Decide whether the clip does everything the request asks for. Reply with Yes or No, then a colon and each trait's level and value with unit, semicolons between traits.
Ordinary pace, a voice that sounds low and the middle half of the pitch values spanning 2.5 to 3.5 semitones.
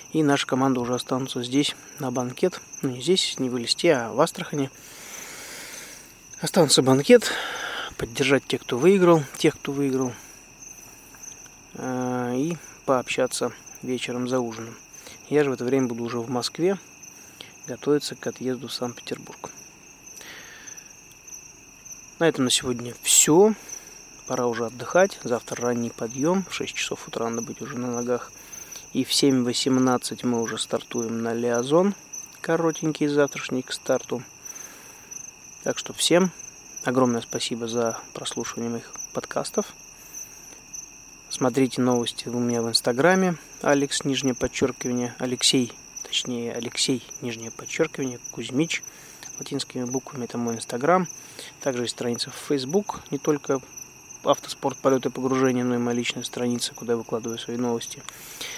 Yes: average, 130 wpm; low, 130 Hz; average, 3.0 semitones